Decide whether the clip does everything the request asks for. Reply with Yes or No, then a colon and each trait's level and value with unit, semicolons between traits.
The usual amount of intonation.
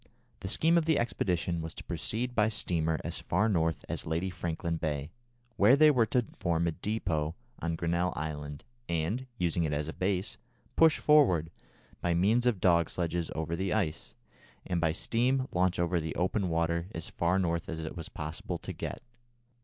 Yes: average, 4.5 semitones